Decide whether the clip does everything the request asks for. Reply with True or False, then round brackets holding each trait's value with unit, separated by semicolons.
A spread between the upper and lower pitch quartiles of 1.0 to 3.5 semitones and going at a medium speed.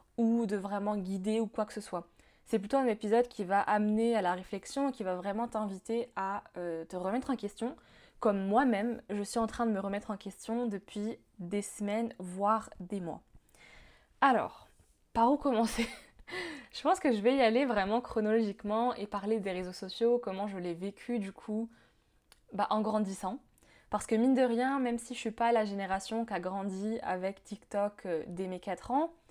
True (2.9 semitones; 195 wpm)